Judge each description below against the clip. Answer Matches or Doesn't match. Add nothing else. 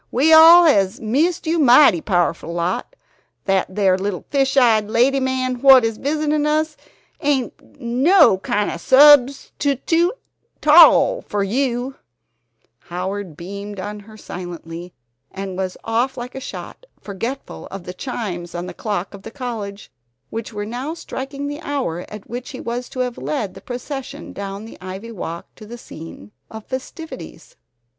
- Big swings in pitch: Matches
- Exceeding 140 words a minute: Matches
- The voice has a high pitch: Matches